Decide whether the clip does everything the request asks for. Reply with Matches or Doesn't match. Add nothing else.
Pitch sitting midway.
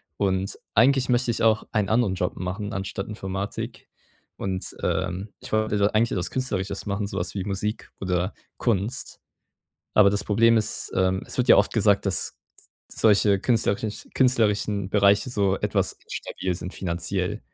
Doesn't match